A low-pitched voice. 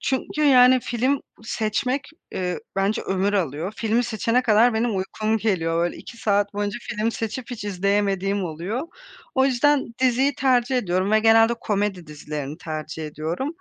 No: high, 215 Hz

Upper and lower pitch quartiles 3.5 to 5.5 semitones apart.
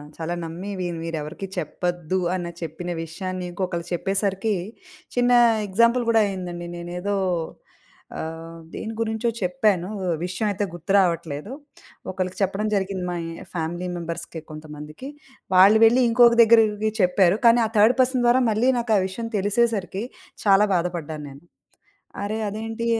Yes: average, 4.1 semitones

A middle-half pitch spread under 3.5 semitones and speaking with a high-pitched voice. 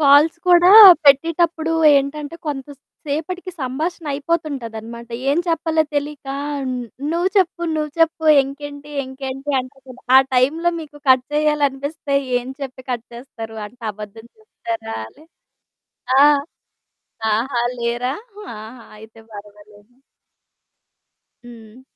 No: average, 4.5 semitones; very high, 275 Hz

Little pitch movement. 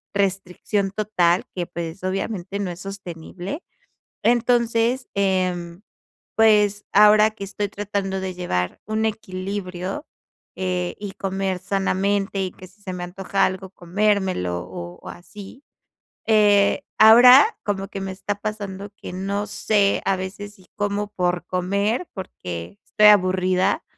Yes: narrow, 2.2 semitones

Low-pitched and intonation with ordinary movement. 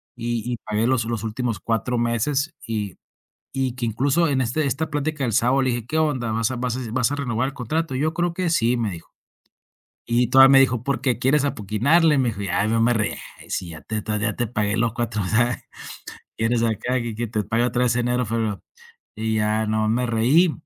Yes: low, 120 Hz; average, 3.2 semitones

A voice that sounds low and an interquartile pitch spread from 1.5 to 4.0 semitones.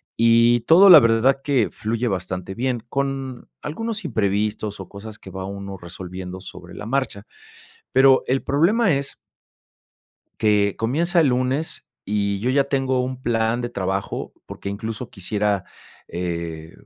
No: low, 115 Hz; average, 5.1 semitones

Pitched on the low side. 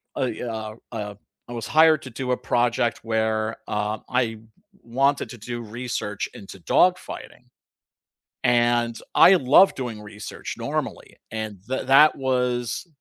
Yes: low, 120 Hz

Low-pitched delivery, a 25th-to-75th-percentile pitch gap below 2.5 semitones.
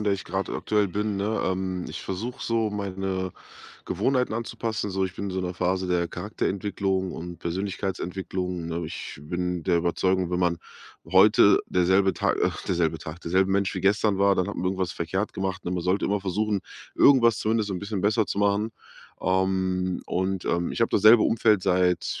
Yes: very low, 95 Hz; narrow, 2.1 semitones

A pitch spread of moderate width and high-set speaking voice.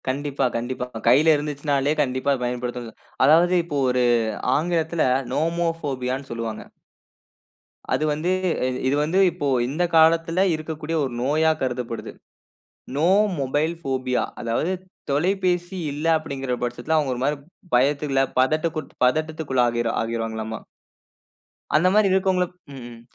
No: average, 4.2 semitones; medium, 145 Hz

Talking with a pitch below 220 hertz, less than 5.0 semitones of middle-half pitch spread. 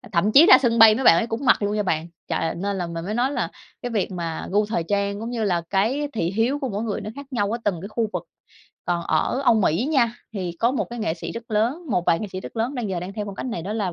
Yes: high, 210 Hz; average, 4.1 semitones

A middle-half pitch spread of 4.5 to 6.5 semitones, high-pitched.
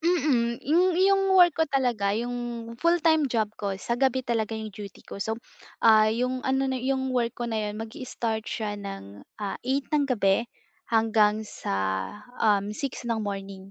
No: average, 3.9 semitones; high, 230 Hz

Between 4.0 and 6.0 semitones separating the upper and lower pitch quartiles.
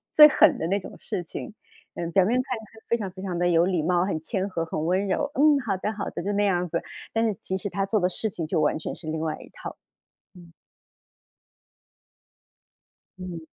No: average, 3.4 semitones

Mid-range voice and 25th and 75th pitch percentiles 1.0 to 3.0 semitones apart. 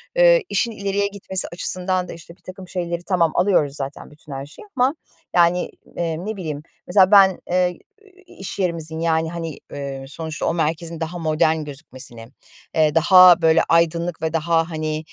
Yes: medium, 170 Hz; average, 2.7 semitones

